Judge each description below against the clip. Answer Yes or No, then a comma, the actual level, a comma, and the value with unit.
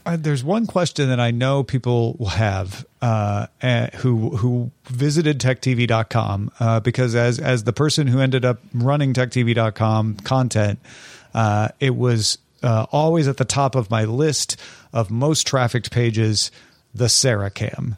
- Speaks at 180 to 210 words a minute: No, average, 145 wpm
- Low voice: Yes, low, 125 Hz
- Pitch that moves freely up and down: No, average, 2.9 semitones